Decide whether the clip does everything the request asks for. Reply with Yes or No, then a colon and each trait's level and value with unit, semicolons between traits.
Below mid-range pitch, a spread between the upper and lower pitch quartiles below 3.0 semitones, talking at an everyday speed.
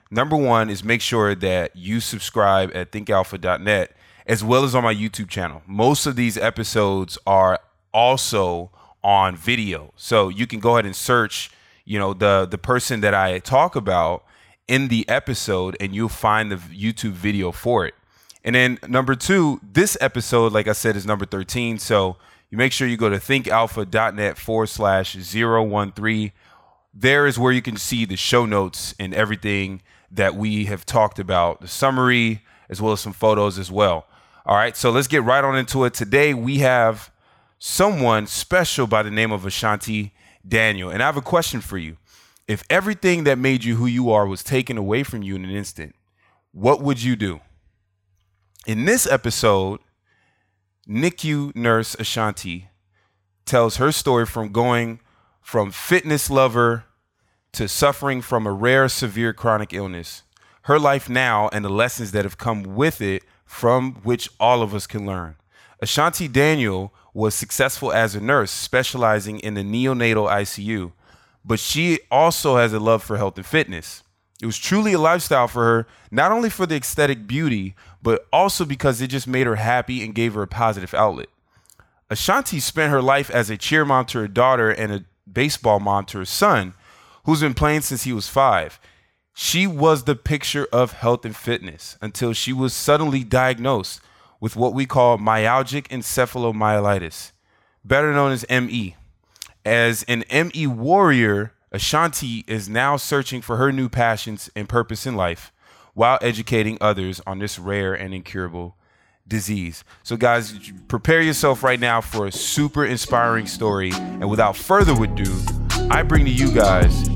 No: low, 115 Hz; average, 4.3 semitones; average, 170 wpm